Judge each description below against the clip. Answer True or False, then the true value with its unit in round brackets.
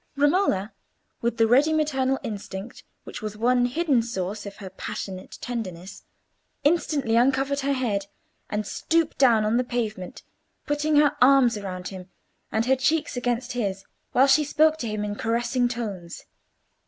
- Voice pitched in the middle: False (240 Hz)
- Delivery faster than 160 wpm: False (155 wpm)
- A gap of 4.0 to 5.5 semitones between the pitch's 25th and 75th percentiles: True (4.7 semitones)